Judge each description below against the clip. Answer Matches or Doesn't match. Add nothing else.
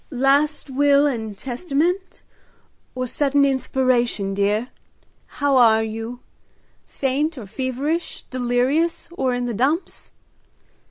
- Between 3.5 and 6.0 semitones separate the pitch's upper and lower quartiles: Doesn't match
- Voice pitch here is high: Matches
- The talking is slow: Matches